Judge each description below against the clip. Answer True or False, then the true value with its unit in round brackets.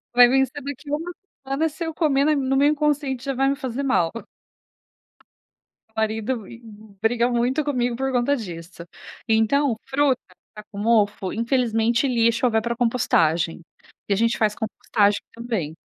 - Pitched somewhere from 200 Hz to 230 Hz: False (240 Hz)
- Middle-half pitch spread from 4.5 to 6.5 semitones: False (3.7 semitones)